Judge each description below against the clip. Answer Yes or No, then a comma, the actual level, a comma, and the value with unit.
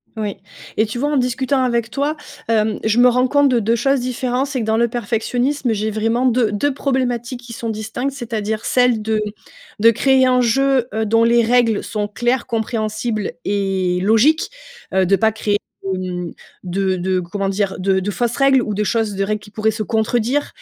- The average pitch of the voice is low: No, high, 225 Hz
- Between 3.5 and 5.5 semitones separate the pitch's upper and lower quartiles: No, average, 3.0 semitones